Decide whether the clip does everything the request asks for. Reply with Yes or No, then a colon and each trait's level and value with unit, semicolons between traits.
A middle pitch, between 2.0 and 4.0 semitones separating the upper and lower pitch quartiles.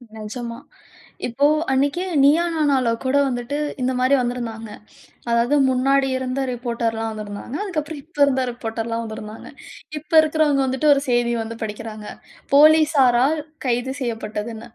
No: very high, 250 Hz; average, 3.5 semitones